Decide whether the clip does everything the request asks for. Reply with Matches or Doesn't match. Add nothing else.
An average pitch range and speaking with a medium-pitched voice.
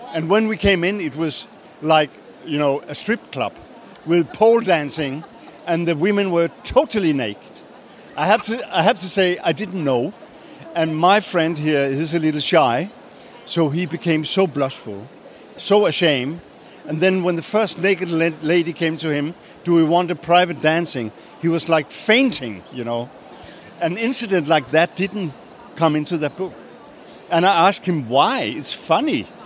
Matches